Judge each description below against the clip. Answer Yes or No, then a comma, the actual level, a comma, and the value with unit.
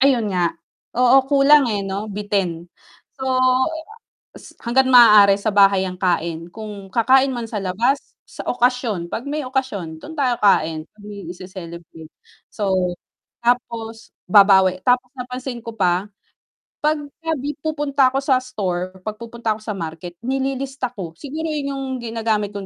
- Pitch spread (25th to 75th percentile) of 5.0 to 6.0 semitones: Yes, wide, 5.4 semitones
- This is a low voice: No, high, 220 Hz